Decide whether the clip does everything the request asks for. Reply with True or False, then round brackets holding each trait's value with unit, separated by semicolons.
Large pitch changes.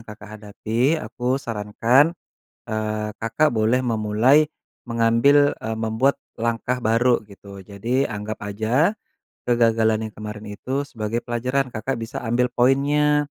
False (3.2 semitones)